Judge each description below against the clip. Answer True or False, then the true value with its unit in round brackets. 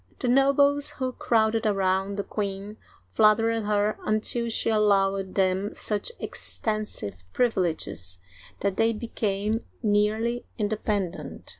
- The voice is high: True (210 Hz)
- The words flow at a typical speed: False (110 wpm)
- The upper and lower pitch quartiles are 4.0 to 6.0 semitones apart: False (2.5 semitones)